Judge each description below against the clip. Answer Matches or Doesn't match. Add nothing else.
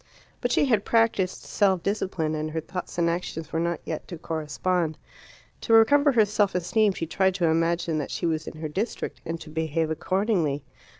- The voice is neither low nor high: Matches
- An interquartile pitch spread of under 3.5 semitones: Doesn't match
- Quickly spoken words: Doesn't match